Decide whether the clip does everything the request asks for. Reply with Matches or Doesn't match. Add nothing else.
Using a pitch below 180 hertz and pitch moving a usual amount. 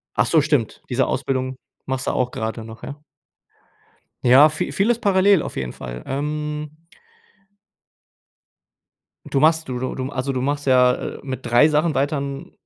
Matches